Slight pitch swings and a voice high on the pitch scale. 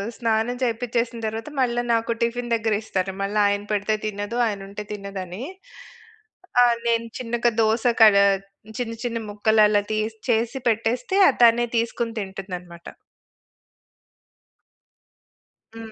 Yes: narrow, 2.3 semitones; high, 225 Hz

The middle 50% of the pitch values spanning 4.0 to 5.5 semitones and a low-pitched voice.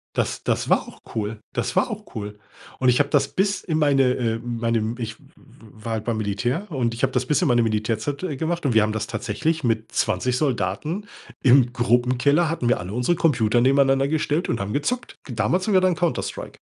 Yes: average, 5.2 semitones; low, 125 Hz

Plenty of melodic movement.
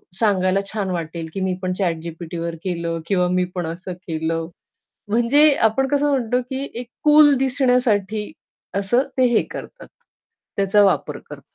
Yes: wide, 6.1 semitones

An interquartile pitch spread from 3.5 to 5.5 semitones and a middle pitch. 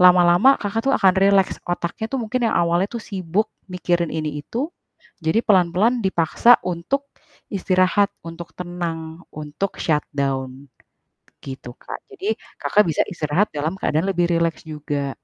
Yes: average, 4.0 semitones; medium, 175 Hz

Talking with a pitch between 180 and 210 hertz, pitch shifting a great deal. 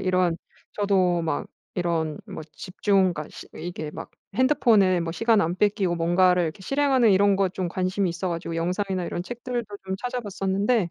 No: medium, 185 Hz; average, 2.9 semitones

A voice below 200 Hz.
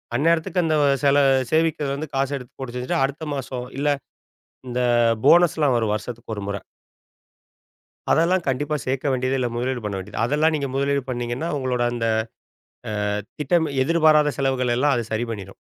Yes: low, 135 Hz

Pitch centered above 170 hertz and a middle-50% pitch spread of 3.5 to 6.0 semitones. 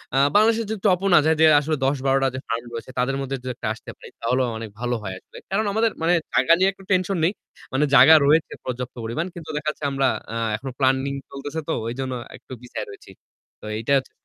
No: low, 135 Hz; average, 4.5 semitones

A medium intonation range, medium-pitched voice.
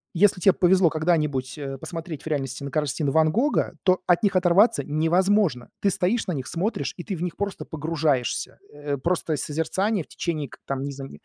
Yes: average, 4.4 semitones; medium, 160 Hz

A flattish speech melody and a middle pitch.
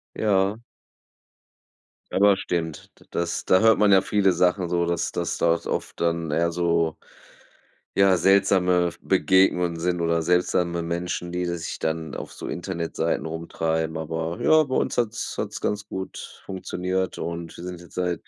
No: narrow, 2.2 semitones; very low, 90 Hz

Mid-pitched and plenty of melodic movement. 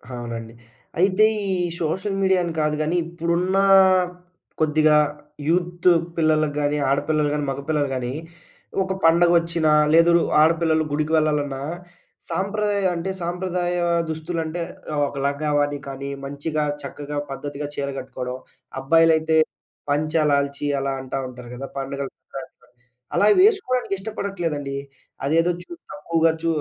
No: medium, 155 Hz; average, 3.3 semitones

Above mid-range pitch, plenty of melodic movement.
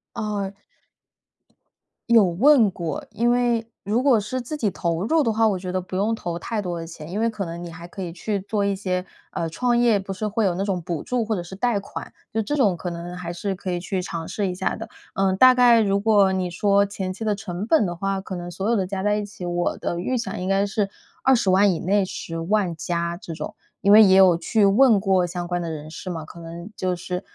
No: high, 195 Hz; average, 3.5 semitones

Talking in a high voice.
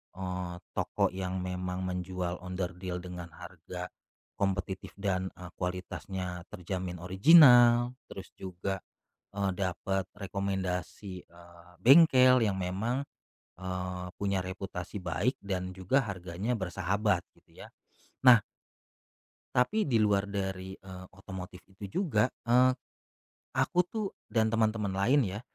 No: very low, 95 Hz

